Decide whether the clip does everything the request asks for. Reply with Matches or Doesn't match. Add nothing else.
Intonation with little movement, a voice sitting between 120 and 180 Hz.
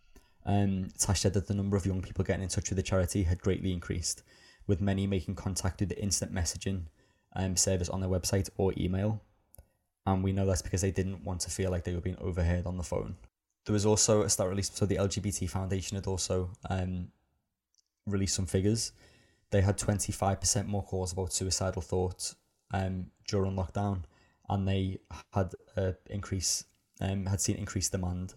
Doesn't match